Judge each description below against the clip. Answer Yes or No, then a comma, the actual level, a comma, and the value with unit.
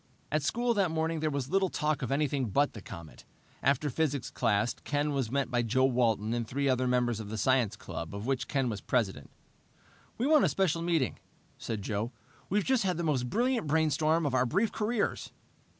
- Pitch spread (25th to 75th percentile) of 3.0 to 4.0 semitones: No, average, 5.2 semitones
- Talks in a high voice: No, medium, 140 Hz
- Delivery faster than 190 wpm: Yes, average, 200 wpm